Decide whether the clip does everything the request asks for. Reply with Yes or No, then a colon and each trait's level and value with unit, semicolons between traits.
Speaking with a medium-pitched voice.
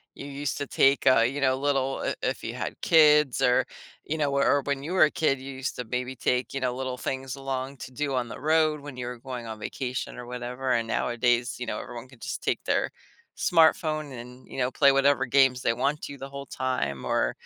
No: low, 130 Hz